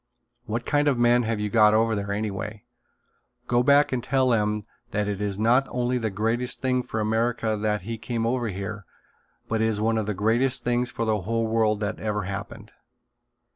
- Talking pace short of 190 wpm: No, average, 200 wpm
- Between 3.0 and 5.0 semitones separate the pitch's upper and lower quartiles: No, narrow, 2.4 semitones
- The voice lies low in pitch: Yes, low, 110 Hz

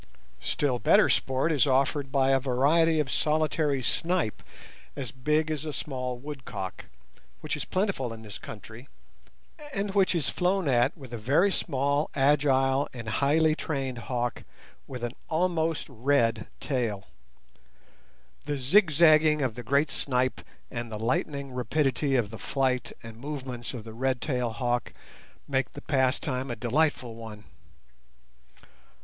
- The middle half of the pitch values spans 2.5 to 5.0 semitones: Yes, average, 3.7 semitones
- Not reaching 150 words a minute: Yes, average, 140 wpm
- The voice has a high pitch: No, low, 135 Hz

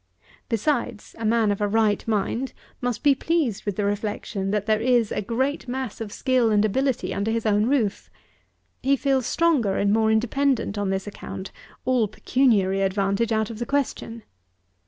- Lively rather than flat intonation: No, average, 3.8 semitones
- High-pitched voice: Yes, high, 225 Hz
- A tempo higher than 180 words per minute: No, average, 175 wpm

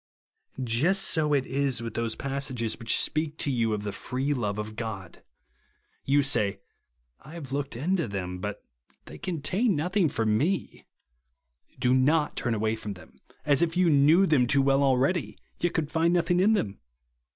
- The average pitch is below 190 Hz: Yes, low, 135 Hz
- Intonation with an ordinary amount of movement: No, wide, 6.0 semitones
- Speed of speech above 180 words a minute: Yes, average, 190 wpm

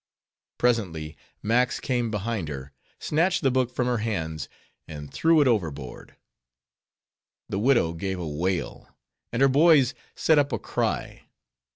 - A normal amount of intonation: No, wide, 8.0 semitones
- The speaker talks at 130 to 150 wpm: Yes, average, 140 wpm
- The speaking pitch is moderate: No, low, 115 Hz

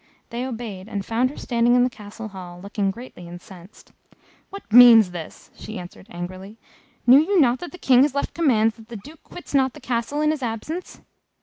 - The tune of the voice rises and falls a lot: No, average, 4.8 semitones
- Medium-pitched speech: No, high, 235 Hz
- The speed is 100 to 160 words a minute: No, average, 200 wpm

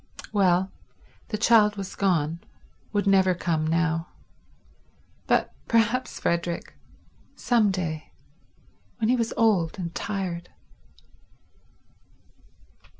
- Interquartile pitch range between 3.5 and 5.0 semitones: Yes, average, 3.8 semitones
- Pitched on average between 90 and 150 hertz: No, high, 190 Hz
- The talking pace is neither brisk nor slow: No, slow, 85 wpm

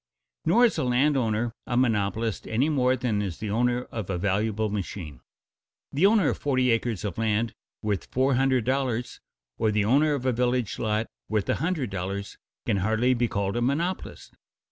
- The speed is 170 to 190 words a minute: Yes, average, 185 wpm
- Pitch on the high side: No, low, 115 Hz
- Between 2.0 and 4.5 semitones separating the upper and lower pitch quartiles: Yes, average, 3.7 semitones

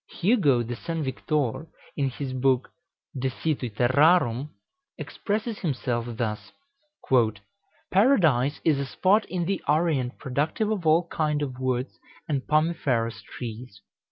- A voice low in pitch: No, medium, 145 Hz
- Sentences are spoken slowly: Yes, slow, 125 wpm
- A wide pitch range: No, average, 4.8 semitones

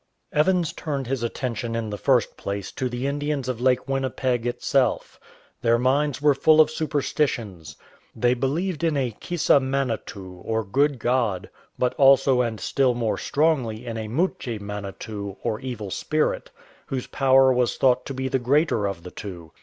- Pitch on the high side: No, low, 125 Hz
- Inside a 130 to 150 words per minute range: No, average, 165 wpm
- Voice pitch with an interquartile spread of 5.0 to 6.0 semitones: No, average, 3.7 semitones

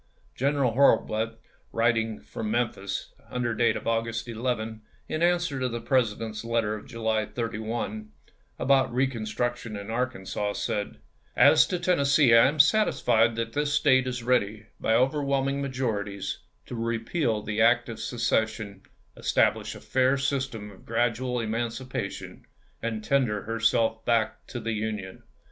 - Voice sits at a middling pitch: No, low, 115 Hz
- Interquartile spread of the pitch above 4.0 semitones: No, average, 2.8 semitones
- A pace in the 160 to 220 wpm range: No, average, 140 wpm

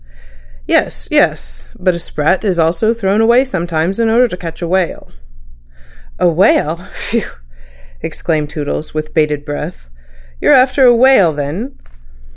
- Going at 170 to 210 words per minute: No, average, 140 wpm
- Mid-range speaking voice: Yes, medium, 175 Hz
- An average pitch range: No, wide, 6.4 semitones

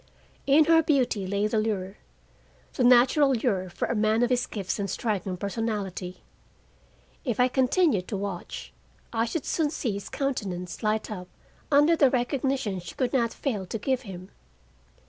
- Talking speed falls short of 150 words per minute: No, average, 165 wpm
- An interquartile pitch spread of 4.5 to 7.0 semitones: Yes, average, 5.0 semitones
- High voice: Yes, high, 225 Hz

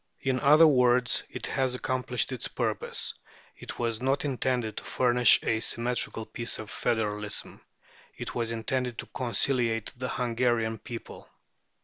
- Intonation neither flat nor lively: No, narrow, 2.0 semitones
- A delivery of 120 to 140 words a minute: Yes, slow, 135 wpm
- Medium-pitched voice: No, low, 120 Hz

